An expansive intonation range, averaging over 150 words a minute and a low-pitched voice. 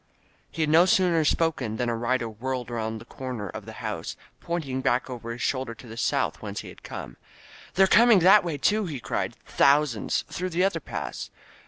Yes: wide, 6.5 semitones; fast, 205 wpm; low, 130 Hz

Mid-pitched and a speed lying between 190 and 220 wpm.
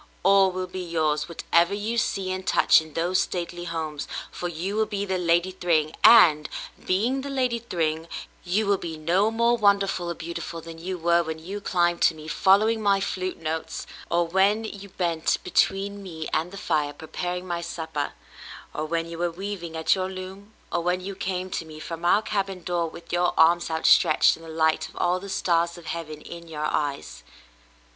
Yes: medium, 175 Hz; average, 200 wpm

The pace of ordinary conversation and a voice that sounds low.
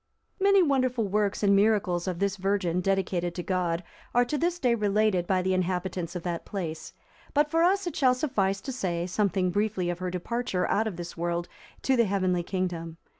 No: average, 195 wpm; high, 195 Hz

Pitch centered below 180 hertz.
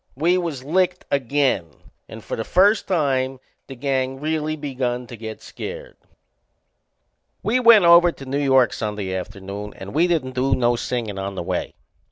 Yes: low, 135 Hz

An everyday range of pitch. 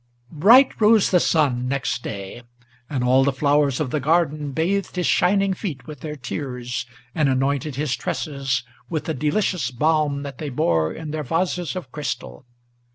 Yes: average, 3.9 semitones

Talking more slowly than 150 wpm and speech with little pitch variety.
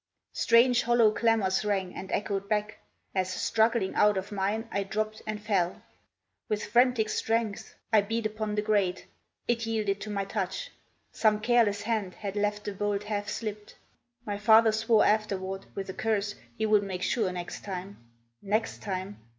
No: average, 165 wpm; narrow, 1.9 semitones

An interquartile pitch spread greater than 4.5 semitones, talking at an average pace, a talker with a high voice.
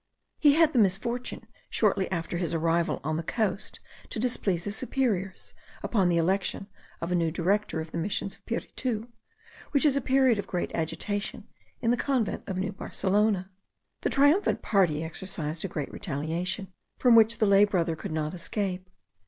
Yes: average, 5.0 semitones; average, 170 wpm; high, 195 Hz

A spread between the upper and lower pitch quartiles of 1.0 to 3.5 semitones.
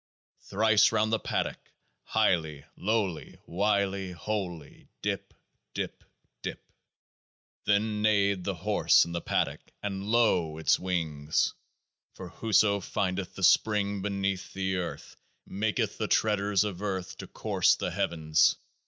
Yes: average, 2.8 semitones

